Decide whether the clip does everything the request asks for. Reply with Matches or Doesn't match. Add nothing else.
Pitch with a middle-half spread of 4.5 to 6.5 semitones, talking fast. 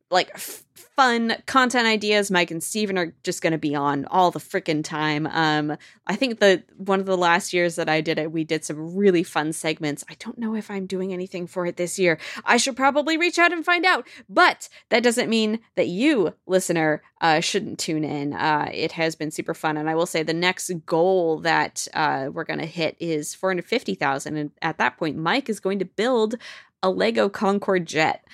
Matches